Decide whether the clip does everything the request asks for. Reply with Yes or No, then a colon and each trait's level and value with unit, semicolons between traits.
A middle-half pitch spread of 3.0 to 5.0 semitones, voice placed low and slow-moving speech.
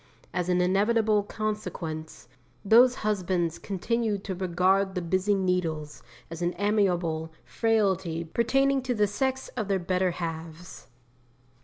No: average, 3.6 semitones; high, 190 Hz; slow, 125 wpm